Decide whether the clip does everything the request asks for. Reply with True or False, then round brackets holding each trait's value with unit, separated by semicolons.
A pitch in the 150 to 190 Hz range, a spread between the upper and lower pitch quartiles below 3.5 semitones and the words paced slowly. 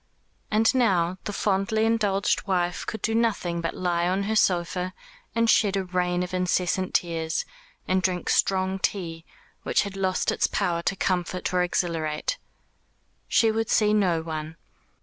False (185 Hz; 2.6 semitones; 155 wpm)